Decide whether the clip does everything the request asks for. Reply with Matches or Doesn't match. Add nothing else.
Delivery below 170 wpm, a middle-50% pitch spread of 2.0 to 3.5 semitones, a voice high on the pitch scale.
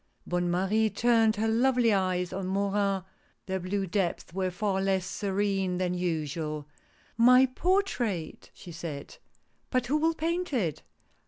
Doesn't match